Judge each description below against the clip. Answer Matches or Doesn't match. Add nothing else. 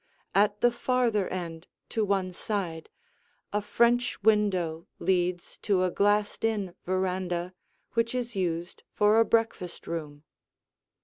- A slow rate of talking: Matches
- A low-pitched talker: Doesn't match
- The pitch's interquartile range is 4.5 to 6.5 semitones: Doesn't match